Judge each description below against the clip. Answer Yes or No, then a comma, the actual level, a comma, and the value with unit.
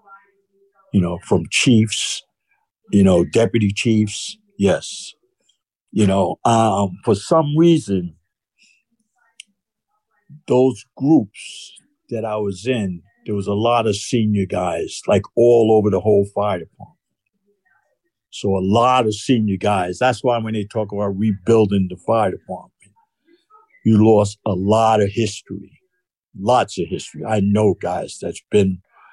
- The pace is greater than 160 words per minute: No, slow, 135 wpm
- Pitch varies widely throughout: Yes, wide, 8.2 semitones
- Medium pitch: No, low, 110 Hz